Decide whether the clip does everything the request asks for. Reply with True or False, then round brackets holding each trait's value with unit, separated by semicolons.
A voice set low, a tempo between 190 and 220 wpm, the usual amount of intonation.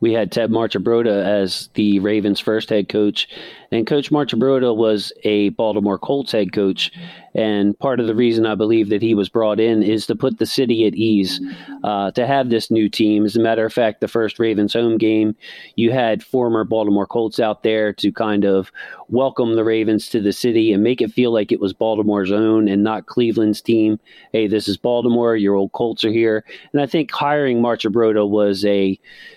False (110 Hz; 200 wpm; 1.9 semitones)